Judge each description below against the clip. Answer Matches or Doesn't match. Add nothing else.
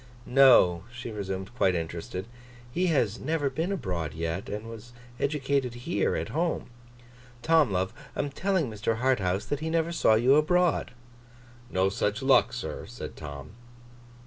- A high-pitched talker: Doesn't match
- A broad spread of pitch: Matches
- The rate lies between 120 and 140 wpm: Doesn't match